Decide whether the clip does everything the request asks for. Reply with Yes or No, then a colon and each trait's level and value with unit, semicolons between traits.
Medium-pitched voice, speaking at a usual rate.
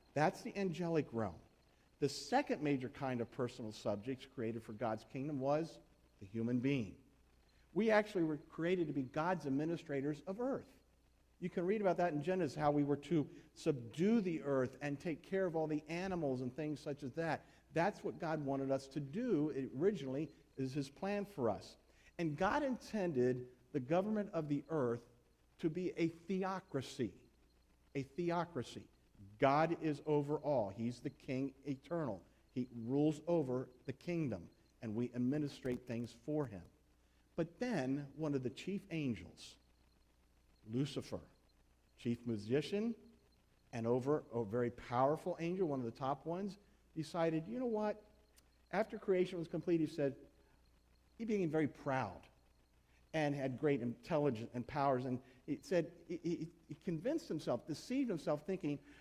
Yes: medium, 145 Hz; average, 155 wpm